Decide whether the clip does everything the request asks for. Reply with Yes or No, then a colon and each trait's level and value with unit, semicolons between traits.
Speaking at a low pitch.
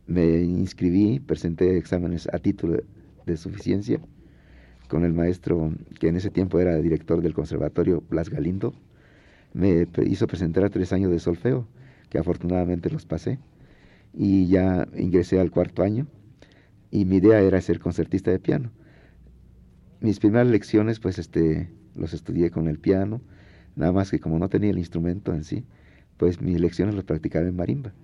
Yes: very low, 90 Hz